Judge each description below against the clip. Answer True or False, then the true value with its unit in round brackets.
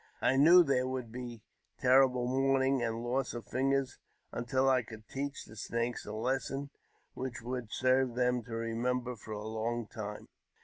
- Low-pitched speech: True (125 Hz)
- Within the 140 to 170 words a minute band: True (165 wpm)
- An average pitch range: False (2.2 semitones)